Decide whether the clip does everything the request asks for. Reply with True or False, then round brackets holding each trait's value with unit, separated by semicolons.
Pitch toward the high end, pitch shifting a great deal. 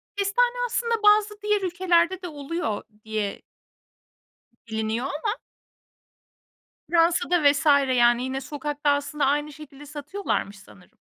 True (300 Hz; 5.9 semitones)